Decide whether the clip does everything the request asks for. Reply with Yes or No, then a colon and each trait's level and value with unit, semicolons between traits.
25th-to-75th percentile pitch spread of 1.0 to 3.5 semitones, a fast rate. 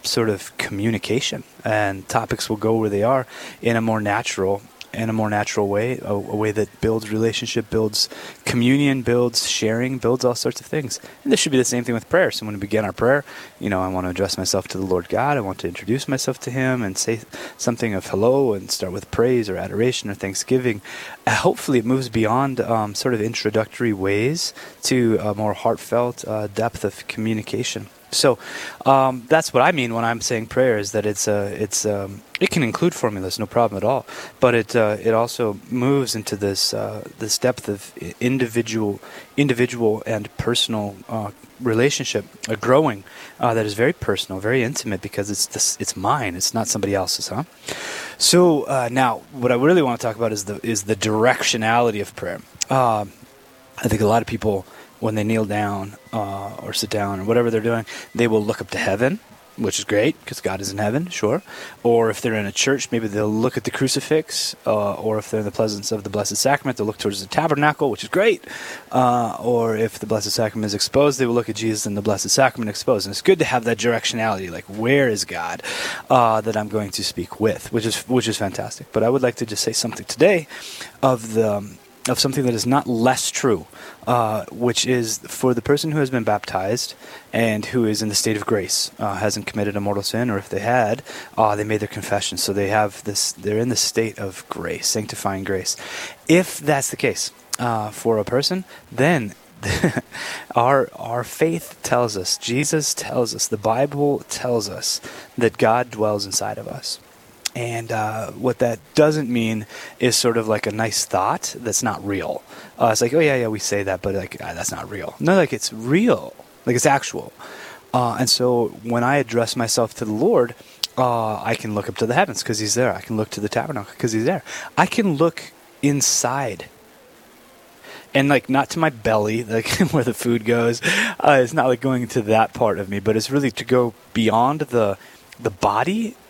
Yes: average, 3.0 semitones; fast, 210 wpm